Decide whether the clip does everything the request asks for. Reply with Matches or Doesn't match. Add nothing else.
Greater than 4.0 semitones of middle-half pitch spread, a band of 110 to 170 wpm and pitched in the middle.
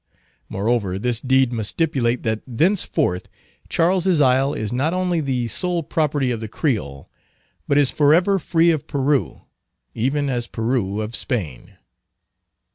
Doesn't match